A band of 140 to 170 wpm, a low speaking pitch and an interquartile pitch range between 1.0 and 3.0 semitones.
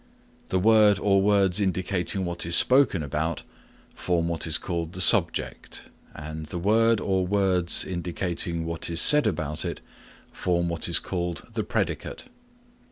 Yes: average, 150 wpm; very low, 90 Hz; average, 2.7 semitones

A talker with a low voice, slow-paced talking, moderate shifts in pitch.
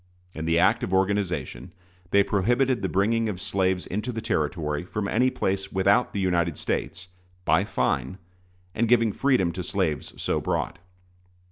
No: very low, 95 Hz; average, 155 wpm; average, 4.2 semitones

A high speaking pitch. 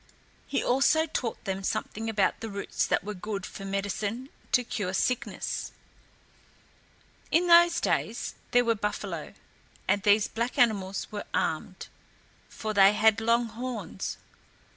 Yes: high, 220 Hz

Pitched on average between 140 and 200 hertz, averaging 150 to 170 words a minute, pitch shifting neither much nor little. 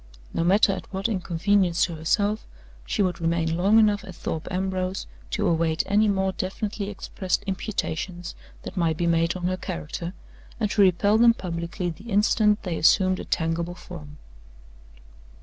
Yes: medium, 185 Hz; average, 160 wpm; average, 3.1 semitones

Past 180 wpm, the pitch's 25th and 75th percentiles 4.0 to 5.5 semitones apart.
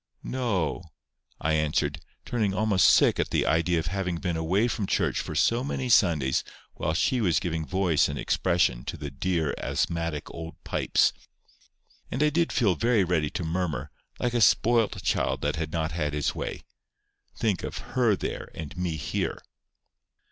No: average, 170 wpm; average, 5.1 semitones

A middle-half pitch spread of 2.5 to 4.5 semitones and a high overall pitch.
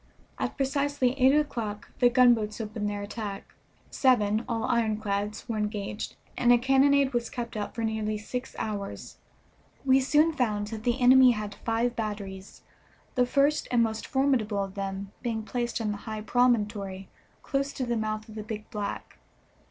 Yes: average, 3.1 semitones; high, 225 Hz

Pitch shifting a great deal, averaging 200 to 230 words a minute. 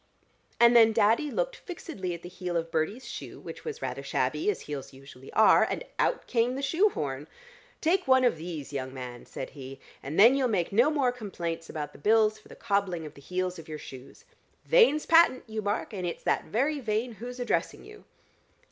Yes: wide, 7.9 semitones; fast, 205 wpm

